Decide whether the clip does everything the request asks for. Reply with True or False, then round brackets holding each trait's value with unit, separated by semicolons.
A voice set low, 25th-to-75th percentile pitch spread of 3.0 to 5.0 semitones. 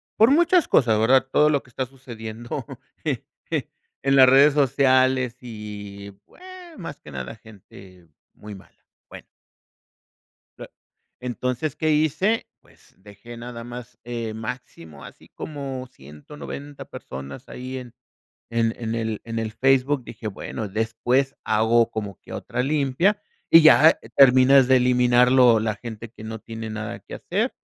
True (120 Hz; 3.5 semitones)